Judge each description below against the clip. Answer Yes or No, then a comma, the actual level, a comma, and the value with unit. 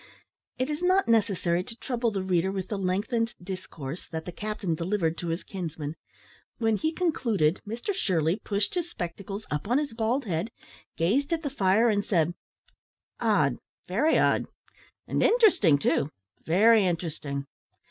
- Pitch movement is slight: No, wide, 5.6 semitones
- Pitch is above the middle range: Yes, high, 200 Hz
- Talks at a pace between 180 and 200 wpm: No, average, 155 wpm